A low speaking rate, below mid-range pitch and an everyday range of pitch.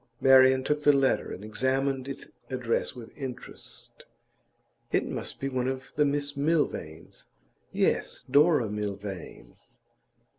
Yes: slow, 120 wpm; low, 130 Hz; average, 3.4 semitones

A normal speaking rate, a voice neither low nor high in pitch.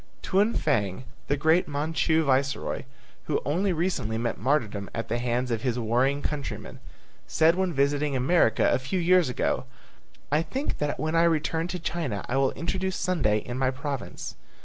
Yes: average, 170 wpm; medium, 145 Hz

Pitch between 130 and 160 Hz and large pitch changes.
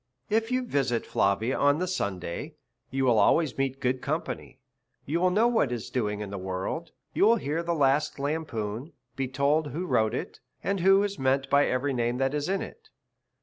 Yes: medium, 140 Hz; wide, 5.7 semitones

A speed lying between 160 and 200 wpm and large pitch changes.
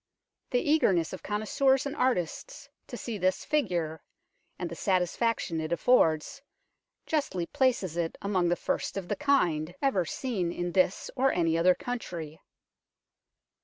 No: average, 140 wpm; wide, 6.8 semitones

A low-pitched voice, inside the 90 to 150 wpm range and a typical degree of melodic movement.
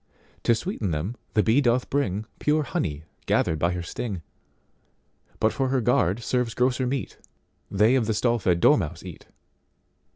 Yes: low, 115 Hz; average, 140 wpm; average, 5.0 semitones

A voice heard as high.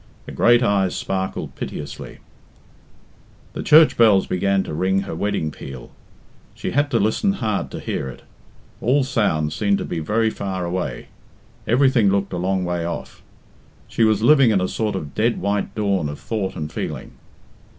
No: low, 100 Hz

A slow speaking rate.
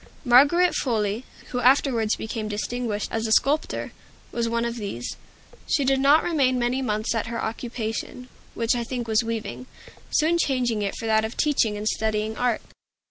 No: average, 170 wpm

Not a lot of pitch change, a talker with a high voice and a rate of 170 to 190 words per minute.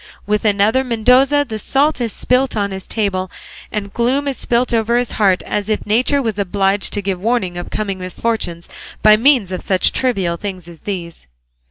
No: average, 4.2 semitones; high, 210 Hz; average, 185 wpm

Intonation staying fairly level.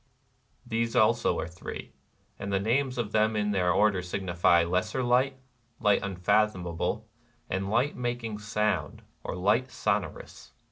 No: average, 4.1 semitones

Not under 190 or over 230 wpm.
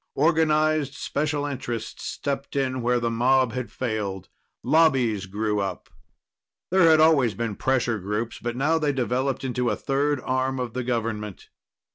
No: average, 150 wpm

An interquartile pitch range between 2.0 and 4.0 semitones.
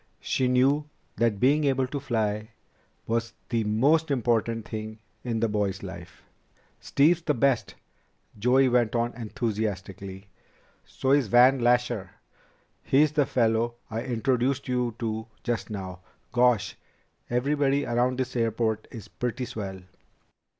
Yes: average, 3.0 semitones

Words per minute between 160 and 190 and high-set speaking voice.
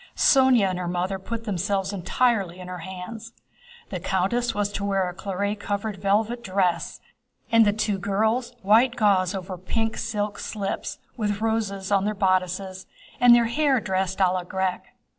Yes: average, 165 wpm; high, 200 Hz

